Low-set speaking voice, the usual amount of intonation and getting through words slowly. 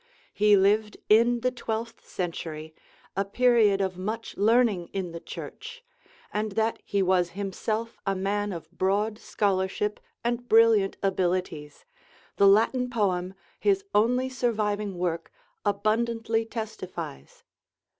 No: high, 205 Hz; average, 3.3 semitones; slow, 120 wpm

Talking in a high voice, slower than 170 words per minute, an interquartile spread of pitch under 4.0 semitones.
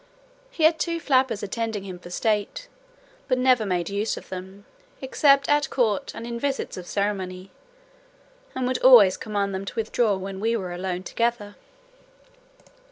No: high, 215 Hz; average, 160 wpm; average, 4.9 semitones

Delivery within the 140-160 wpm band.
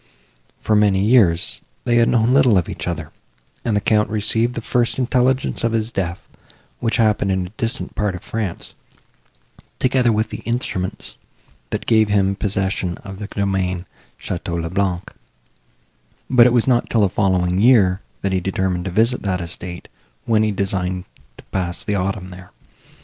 No: average, 170 wpm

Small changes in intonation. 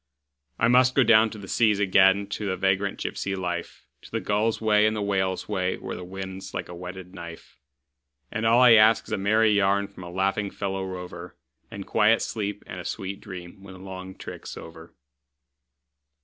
Yes: narrow, 2.3 semitones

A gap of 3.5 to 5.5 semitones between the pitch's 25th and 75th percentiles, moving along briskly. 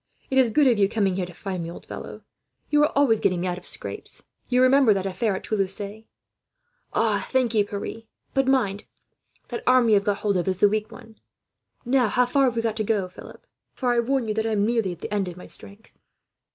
Yes: average, 4.0 semitones; fast, 230 wpm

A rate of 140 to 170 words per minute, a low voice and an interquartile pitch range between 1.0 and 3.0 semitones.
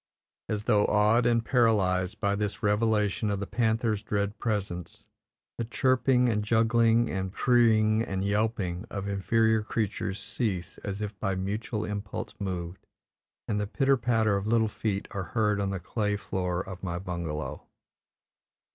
Yes: average, 165 wpm; low, 105 Hz; narrow, 2.6 semitones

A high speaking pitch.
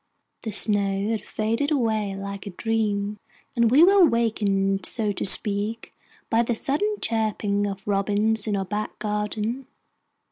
Yes: high, 215 Hz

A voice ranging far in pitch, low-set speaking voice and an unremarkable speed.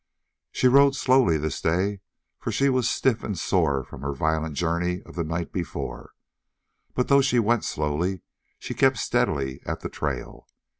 Yes: wide, 7.8 semitones; very low, 90 Hz; average, 165 wpm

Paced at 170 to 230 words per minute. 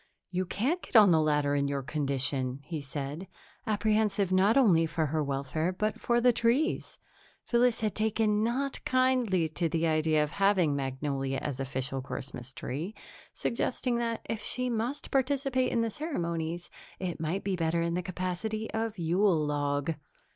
No: average, 160 wpm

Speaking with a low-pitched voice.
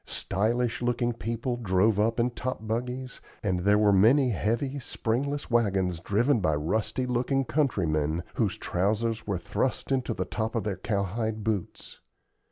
Yes: low, 110 Hz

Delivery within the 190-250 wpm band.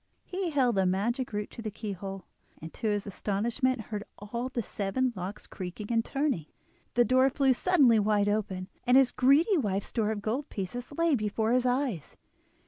No: average, 180 wpm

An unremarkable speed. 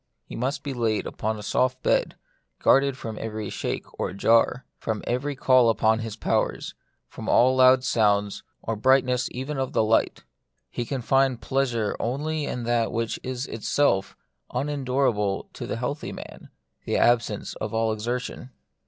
Yes: average, 160 wpm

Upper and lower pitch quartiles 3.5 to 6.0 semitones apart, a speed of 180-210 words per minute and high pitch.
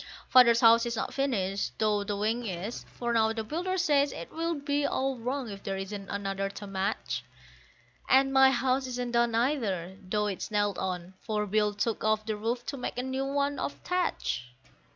Yes: average, 4.6 semitones; average, 195 wpm; high, 230 Hz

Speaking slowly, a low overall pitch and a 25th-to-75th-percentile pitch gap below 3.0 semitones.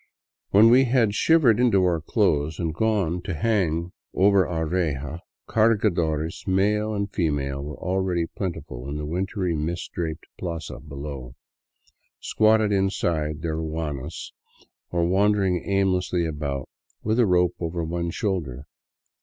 No: slow, 130 wpm; very low, 85 Hz; average, 4.2 semitones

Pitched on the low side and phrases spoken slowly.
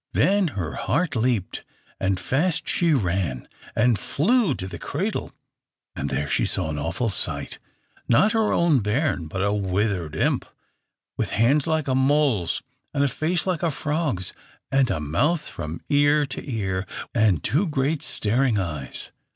No: low, 125 Hz; average, 160 wpm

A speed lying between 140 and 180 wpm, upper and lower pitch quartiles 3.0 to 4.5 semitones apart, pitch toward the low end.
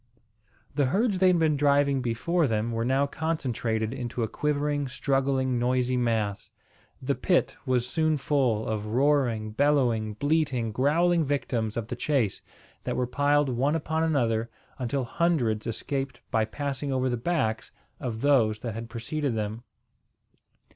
Yes: average, 145 wpm; average, 4.1 semitones; low, 130 Hz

